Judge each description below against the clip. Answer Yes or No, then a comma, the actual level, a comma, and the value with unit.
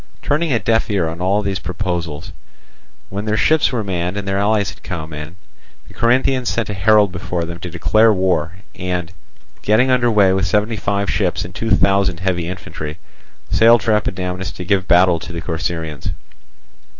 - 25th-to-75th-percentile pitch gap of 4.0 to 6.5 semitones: No, average, 3.4 semitones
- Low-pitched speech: Yes, very low, 95 Hz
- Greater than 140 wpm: Yes, average, 180 wpm